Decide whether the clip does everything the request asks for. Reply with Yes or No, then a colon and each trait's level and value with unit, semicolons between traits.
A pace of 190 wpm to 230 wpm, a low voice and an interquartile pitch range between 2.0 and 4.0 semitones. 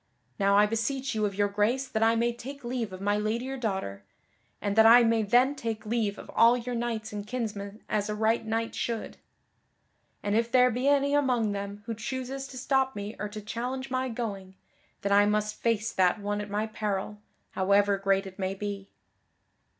No: average, 200 wpm; high, 220 Hz; average, 3.0 semitones